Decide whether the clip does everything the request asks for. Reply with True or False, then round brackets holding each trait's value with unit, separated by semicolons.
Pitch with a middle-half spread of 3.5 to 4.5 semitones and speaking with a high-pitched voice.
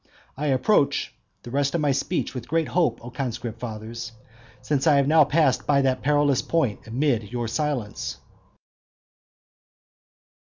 False (3.9 semitones; 135 Hz)